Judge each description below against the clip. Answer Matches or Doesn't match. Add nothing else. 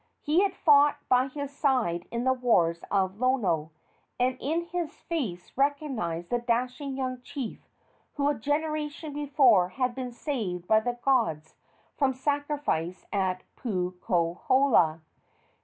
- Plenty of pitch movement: Matches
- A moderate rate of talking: Doesn't match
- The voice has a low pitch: Doesn't match